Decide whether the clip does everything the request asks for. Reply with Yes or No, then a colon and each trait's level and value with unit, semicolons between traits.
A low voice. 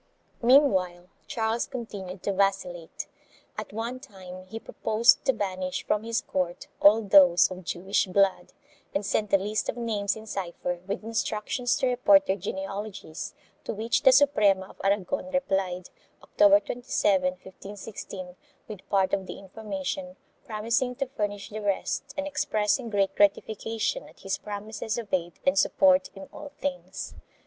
No: high, 205 Hz